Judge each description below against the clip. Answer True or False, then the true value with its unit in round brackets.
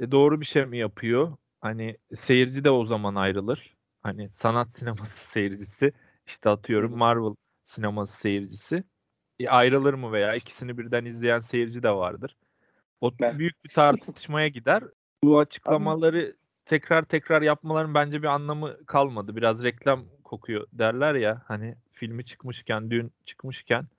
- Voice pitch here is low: True (120 Hz)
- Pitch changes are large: False (4.7 semitones)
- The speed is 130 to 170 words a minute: True (140 wpm)